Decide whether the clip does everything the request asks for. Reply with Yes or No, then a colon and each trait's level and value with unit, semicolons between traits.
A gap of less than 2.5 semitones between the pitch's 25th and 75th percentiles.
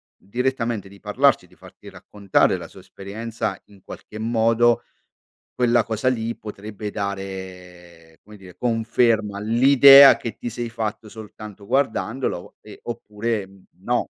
No: average, 2.8 semitones